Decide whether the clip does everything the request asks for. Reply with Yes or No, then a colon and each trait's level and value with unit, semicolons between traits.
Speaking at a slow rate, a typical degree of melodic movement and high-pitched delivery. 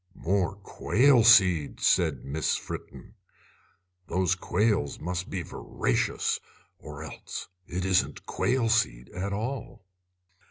No: slow, 110 wpm; average, 4.1 semitones; very low, 95 Hz